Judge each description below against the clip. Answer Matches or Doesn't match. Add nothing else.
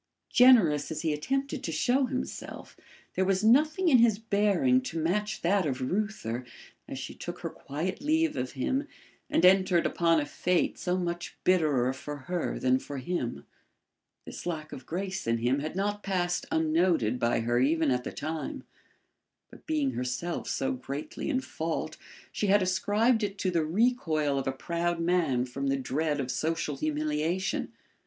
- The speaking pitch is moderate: Matches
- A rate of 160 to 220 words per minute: Matches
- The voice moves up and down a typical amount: Doesn't match